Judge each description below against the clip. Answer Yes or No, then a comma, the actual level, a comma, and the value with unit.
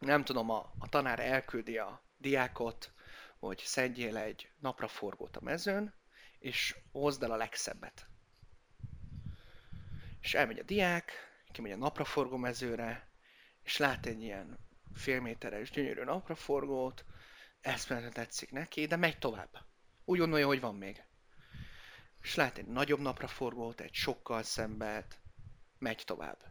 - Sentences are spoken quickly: No, average, 130 wpm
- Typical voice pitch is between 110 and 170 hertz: Yes, low, 125 Hz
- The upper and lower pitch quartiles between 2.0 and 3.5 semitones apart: No, average, 4.1 semitones